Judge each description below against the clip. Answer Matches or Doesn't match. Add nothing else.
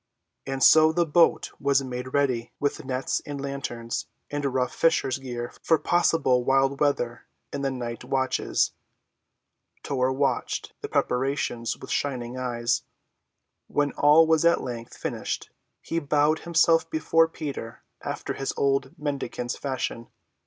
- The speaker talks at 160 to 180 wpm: Doesn't match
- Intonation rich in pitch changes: Doesn't match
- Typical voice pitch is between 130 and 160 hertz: Matches